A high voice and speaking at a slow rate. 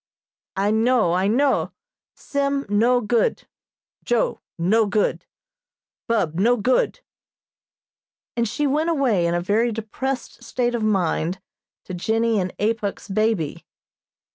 Yes: high, 225 Hz; slow, 120 wpm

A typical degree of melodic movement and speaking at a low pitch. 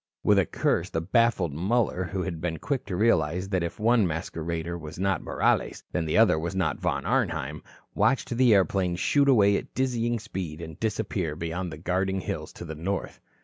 Yes: average, 4.5 semitones; very low, 95 Hz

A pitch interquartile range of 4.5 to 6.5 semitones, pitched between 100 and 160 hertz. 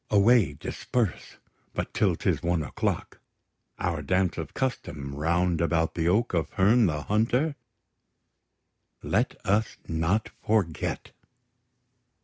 No: average, 5.2 semitones; very low, 90 Hz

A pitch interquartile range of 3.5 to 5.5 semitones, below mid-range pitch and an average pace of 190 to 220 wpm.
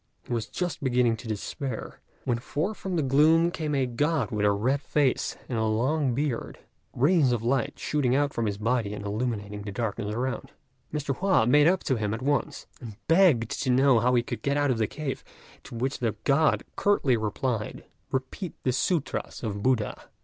Yes: average, 4.4 semitones; low, 130 Hz; average, 195 wpm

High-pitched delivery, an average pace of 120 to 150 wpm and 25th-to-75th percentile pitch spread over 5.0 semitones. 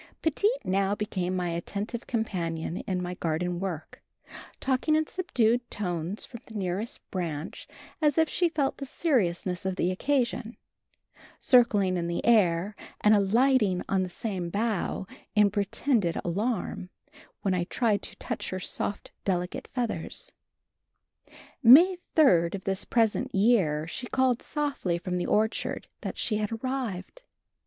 Yes: high, 205 Hz; average, 140 wpm; wide, 5.4 semitones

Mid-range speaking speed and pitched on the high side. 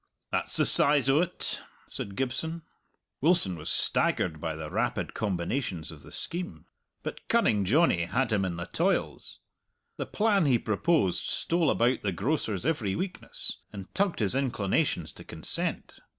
No: average, 150 wpm; low, 120 Hz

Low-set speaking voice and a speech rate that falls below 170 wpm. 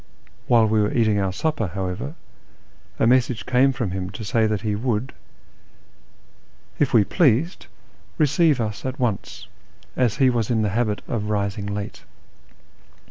Yes: low, 110 Hz; average, 155 wpm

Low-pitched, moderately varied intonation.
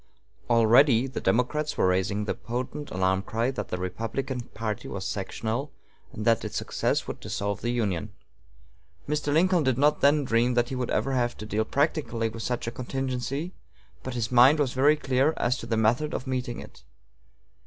Yes: low, 120 Hz; average, 3.6 semitones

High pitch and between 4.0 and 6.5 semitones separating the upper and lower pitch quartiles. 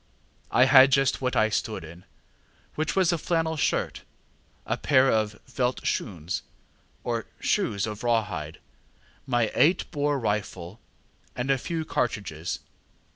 No: low, 125 Hz; average, 5.2 semitones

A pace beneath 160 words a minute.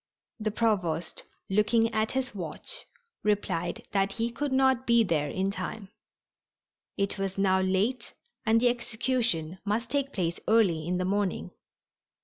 Yes: average, 140 wpm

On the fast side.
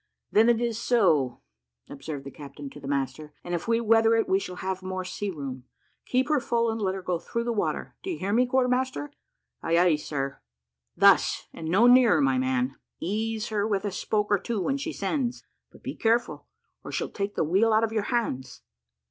Yes: fast, 210 wpm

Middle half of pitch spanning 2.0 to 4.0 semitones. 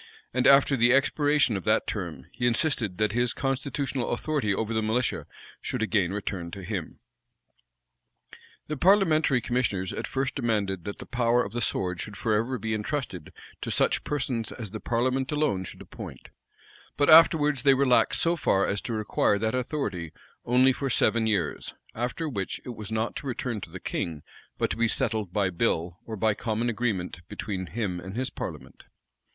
No: average, 4.8 semitones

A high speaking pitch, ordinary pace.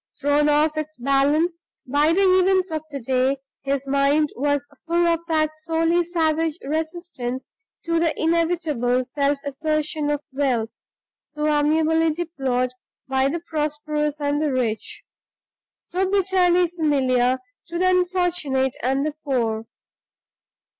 No: very high, 300 Hz; slow, 125 wpm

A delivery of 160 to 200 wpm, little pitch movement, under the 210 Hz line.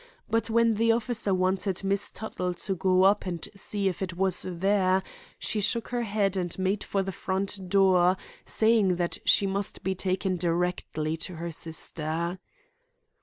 Yes: average, 165 wpm; narrow, 2.1 semitones; high, 190 Hz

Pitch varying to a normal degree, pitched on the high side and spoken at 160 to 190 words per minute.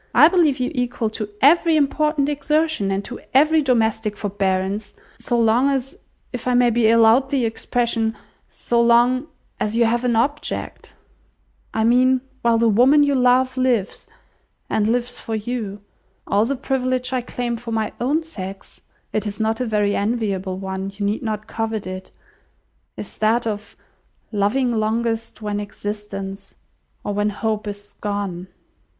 No: average, 3.5 semitones; high, 230 Hz; average, 150 wpm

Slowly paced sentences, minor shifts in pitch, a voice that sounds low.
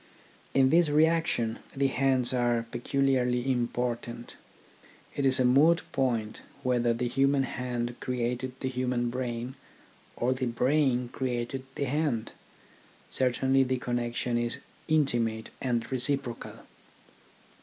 Yes: slow, 120 wpm; narrow, 2.0 semitones; low, 125 Hz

